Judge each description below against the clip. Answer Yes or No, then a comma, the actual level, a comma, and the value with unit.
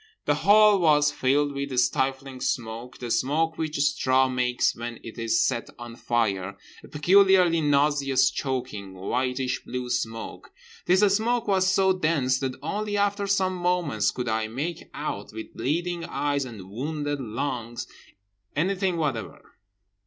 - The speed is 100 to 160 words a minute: Yes, average, 140 wpm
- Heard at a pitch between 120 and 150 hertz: Yes, medium, 140 Hz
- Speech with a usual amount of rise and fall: No, wide, 5.9 semitones